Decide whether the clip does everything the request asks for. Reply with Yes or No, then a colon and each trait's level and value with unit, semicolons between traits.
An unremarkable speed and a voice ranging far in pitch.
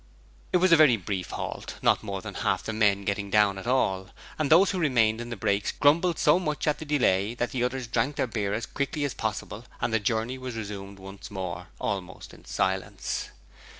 No: fast, 215 wpm; wide, 6.2 semitones